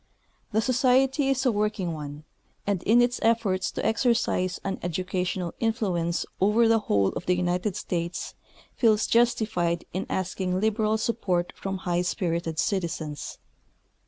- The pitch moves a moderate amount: Yes, average, 4.2 semitones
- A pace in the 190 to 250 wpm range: No, average, 145 wpm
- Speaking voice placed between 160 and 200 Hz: Yes, high, 190 Hz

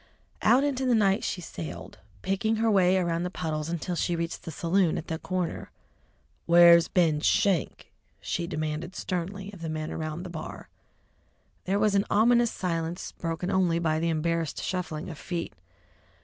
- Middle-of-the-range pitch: Yes, medium, 175 Hz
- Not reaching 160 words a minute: No, average, 165 wpm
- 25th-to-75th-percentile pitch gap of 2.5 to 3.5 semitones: Yes, average, 2.9 semitones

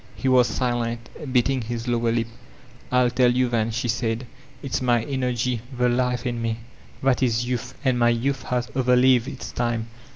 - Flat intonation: Yes, narrow, 1.4 semitones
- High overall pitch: No, low, 120 Hz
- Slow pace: No, average, 185 wpm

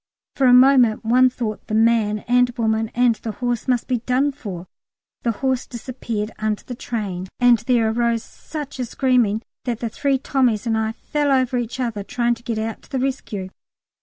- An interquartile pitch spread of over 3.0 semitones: No, narrow, 2.5 semitones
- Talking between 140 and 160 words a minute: No, average, 195 wpm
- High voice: Yes, high, 235 Hz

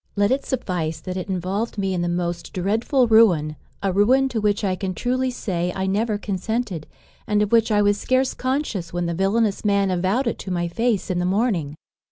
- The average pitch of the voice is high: Yes, high, 200 Hz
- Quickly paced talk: Yes, fast, 210 wpm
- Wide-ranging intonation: No, average, 4.0 semitones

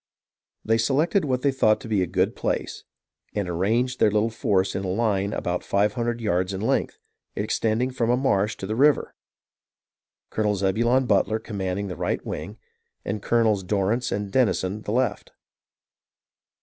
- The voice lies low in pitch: Yes, low, 110 Hz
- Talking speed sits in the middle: Yes, average, 165 wpm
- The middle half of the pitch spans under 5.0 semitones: Yes, average, 3.3 semitones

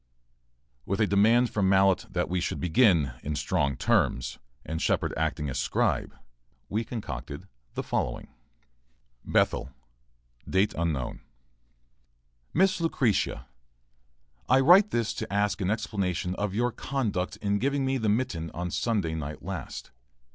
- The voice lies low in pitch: Yes, low, 100 Hz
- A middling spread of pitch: No, wide, 6.0 semitones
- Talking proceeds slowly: Yes, slow, 130 wpm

